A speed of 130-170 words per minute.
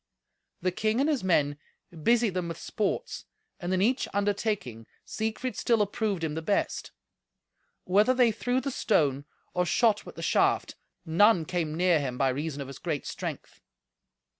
Yes: average, 165 wpm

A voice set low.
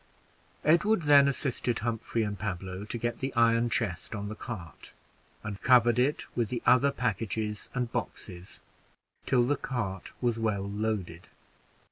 Yes: low, 115 Hz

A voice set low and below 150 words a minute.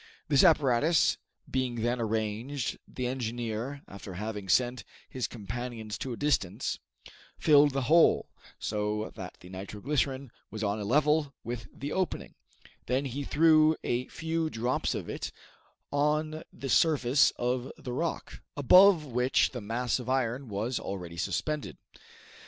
Yes: low, 125 Hz; average, 140 wpm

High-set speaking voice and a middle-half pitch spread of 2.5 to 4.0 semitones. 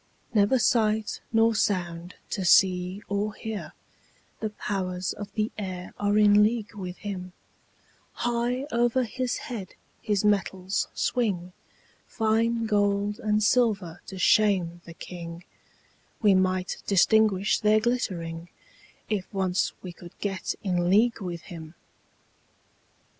Yes: high, 205 Hz; average, 3.1 semitones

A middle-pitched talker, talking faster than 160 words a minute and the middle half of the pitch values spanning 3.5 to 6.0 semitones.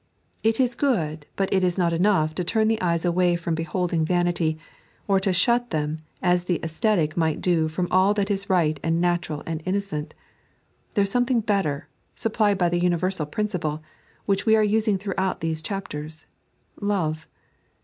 Yes: medium, 180 Hz; average, 175 wpm; average, 3.9 semitones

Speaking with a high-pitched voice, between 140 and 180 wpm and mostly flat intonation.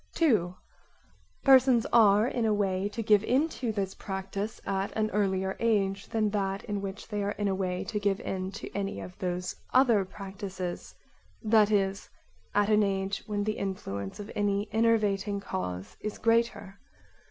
Yes: high, 200 Hz; average, 165 wpm; narrow, 1.9 semitones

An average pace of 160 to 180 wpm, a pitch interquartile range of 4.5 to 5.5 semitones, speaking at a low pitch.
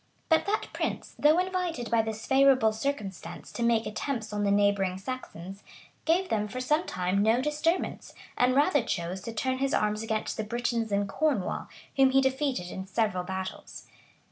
No: average, 170 wpm; average, 5.1 semitones; high, 230 Hz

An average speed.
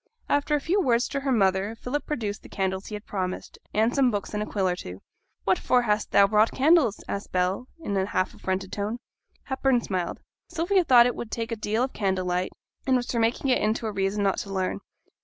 No: fast, 225 wpm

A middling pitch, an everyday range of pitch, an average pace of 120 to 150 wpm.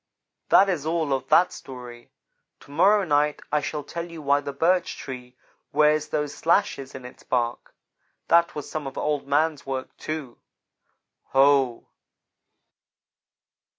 Yes: medium, 145 Hz; average, 3.0 semitones; average, 140 wpm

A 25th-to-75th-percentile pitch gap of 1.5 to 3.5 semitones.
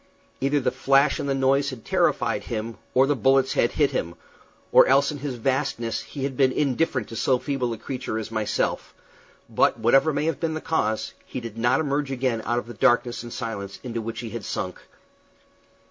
Yes: average, 3.2 semitones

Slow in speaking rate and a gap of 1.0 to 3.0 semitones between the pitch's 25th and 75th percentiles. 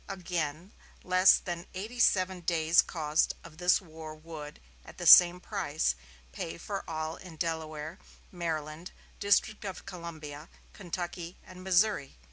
Yes: slow, 130 wpm; average, 2.7 semitones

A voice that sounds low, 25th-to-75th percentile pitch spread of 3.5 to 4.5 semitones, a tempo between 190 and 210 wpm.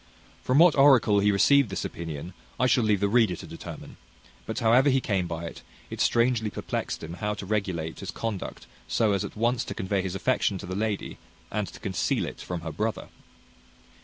Yes: low, 105 Hz; average, 4.1 semitones; average, 200 wpm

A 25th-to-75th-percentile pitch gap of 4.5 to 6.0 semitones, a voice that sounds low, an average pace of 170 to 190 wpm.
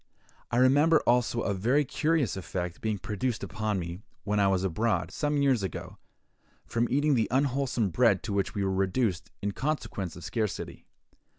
Yes: average, 5.1 semitones; low, 110 Hz; average, 175 wpm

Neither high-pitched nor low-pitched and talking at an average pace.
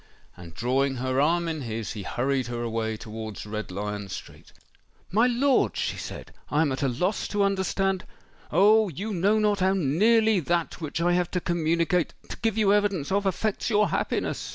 Yes: medium, 170 Hz; average, 175 wpm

